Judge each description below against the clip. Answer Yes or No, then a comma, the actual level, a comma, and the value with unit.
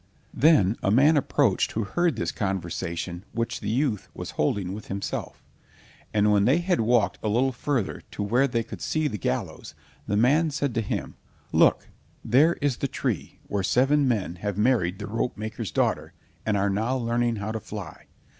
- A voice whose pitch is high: No, low, 115 Hz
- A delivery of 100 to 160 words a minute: No, average, 180 wpm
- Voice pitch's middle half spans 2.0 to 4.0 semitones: No, average, 4.6 semitones